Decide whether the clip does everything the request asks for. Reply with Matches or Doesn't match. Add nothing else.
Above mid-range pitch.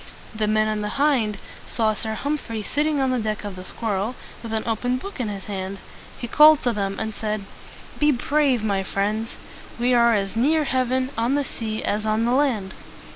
Matches